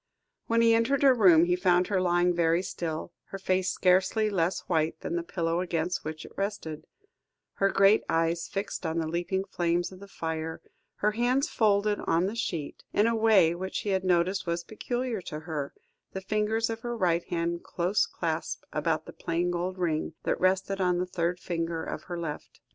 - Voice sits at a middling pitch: Yes, medium, 180 Hz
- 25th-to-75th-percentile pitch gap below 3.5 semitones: Yes, average, 3.0 semitones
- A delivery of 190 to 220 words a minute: Yes, average, 195 wpm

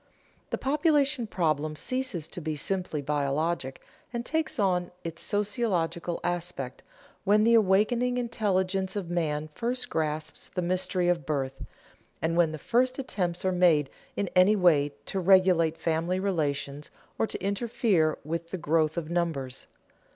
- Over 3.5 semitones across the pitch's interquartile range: Yes, average, 4.6 semitones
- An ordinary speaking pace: Yes, average, 145 wpm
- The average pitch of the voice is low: No, medium, 175 Hz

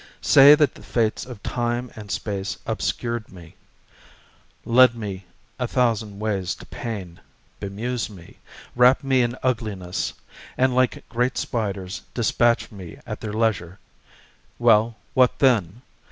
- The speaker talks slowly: Yes, slow, 130 wpm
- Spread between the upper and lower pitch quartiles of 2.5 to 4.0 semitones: Yes, average, 3.7 semitones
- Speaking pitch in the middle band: No, low, 115 Hz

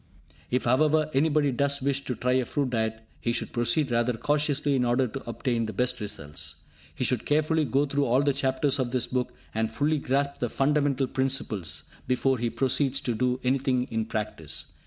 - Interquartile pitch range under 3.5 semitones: Yes, average, 3.0 semitones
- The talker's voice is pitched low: Yes, low, 130 Hz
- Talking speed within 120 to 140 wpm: No, average, 190 wpm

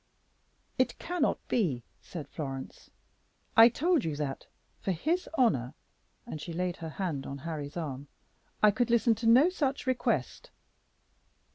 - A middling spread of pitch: No, wide, 9.0 semitones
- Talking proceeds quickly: No, average, 140 wpm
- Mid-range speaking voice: Yes, medium, 180 Hz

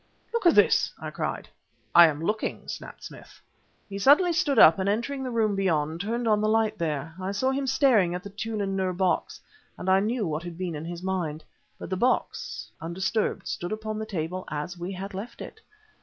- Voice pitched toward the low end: No, high, 195 Hz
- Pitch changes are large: No, average, 4.2 semitones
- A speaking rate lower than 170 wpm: No, fast, 205 wpm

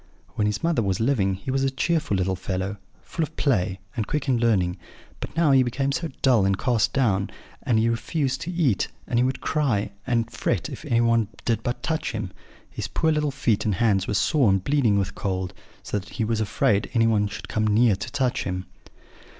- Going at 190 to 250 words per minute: Yes, fast, 205 wpm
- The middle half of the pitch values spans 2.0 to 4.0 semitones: No, average, 5.1 semitones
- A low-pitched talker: Yes, low, 115 Hz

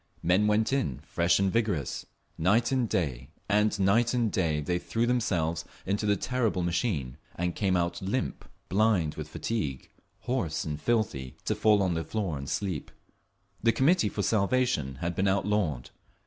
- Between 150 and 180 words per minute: Yes, average, 160 wpm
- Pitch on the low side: Yes, very low, 95 Hz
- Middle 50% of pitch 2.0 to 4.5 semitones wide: No, average, 5.2 semitones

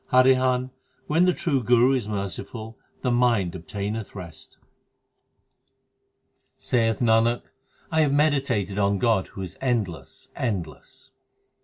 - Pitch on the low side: Yes, low, 115 Hz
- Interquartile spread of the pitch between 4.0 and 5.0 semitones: Yes, average, 4.4 semitones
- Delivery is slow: Yes, slow, 120 wpm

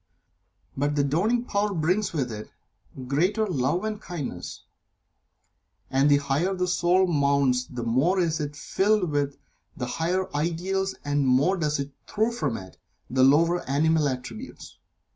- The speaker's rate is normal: Yes, average, 150 wpm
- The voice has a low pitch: No, medium, 155 Hz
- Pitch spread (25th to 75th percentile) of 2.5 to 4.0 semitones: No, average, 5.0 semitones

